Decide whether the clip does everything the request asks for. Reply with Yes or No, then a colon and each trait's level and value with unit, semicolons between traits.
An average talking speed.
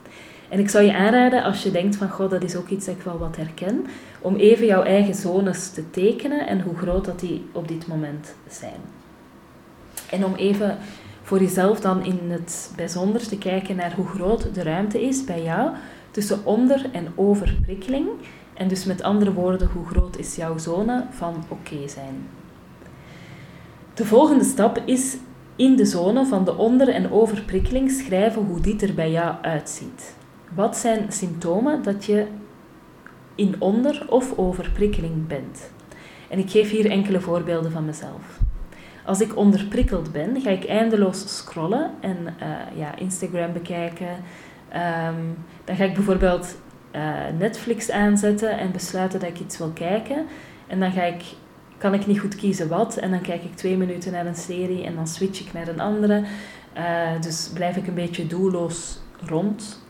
Yes: average, 170 wpm